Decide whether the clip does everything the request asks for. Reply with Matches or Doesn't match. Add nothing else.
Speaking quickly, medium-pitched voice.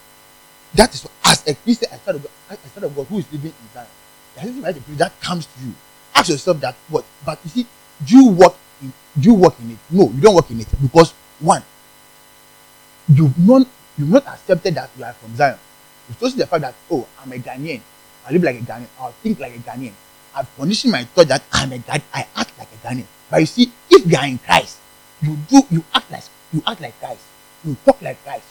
Matches